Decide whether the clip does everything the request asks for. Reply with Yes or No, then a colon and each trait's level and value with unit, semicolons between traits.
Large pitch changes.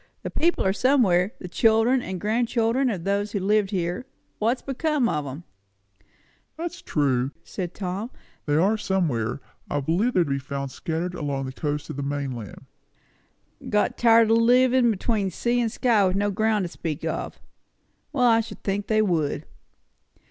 Yes: wide, 6.2 semitones